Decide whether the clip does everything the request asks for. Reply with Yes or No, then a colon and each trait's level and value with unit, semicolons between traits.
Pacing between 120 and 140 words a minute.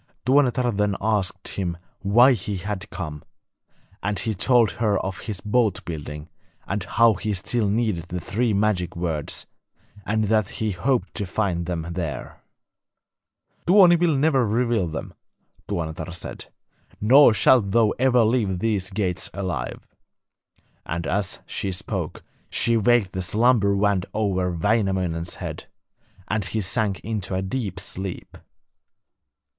Yes: slow, 135 wpm